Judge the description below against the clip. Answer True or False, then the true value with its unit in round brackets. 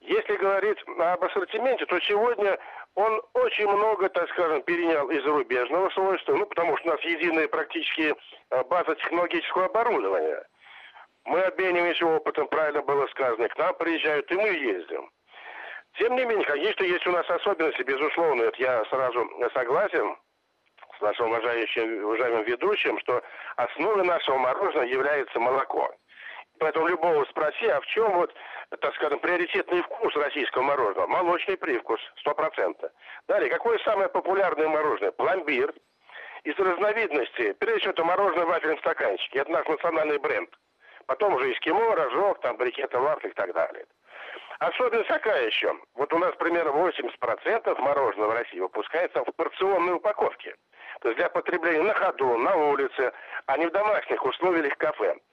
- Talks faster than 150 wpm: False (145 wpm)